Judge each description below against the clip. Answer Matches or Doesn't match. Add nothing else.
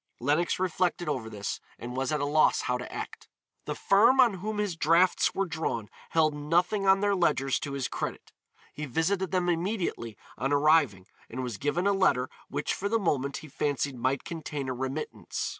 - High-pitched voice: Doesn't match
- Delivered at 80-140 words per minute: Doesn't match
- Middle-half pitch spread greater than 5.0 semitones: Matches